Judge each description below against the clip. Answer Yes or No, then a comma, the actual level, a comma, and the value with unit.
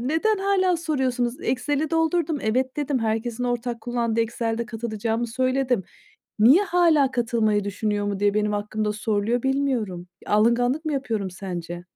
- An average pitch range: Yes, average, 4.3 semitones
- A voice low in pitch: No, high, 240 Hz